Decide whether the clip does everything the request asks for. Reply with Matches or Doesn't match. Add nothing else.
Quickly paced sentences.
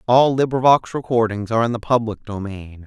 Doesn't match